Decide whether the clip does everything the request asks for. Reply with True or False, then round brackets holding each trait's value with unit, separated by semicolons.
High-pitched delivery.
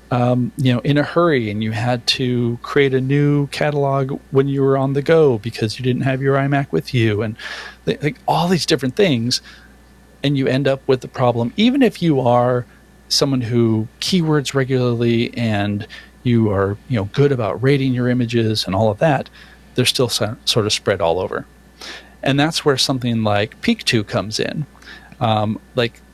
False (125 Hz)